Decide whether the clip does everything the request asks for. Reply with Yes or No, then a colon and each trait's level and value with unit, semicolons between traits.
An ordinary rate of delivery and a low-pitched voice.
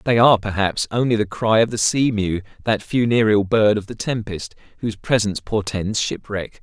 Yes: average, 180 wpm; low, 105 Hz